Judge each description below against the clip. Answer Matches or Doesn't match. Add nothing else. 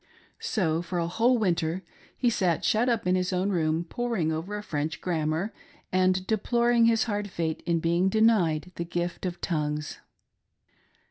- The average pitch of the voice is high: Doesn't match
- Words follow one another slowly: Doesn't match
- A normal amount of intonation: Matches